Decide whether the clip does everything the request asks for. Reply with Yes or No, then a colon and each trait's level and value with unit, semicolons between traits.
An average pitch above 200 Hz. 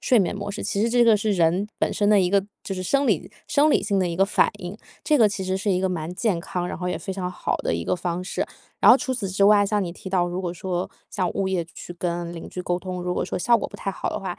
No: high, 190 Hz